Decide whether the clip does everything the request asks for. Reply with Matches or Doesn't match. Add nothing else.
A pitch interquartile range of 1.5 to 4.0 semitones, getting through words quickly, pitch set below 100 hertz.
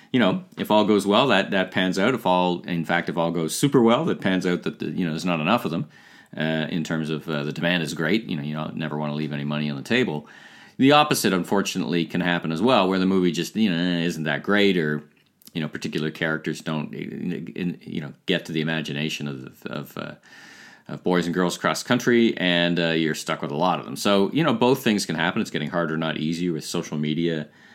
Matches